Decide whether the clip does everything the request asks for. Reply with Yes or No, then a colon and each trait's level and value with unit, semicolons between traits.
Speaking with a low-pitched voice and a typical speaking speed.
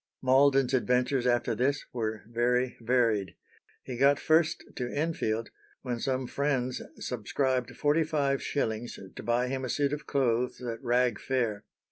Yes: low, 125 Hz; average, 145 wpm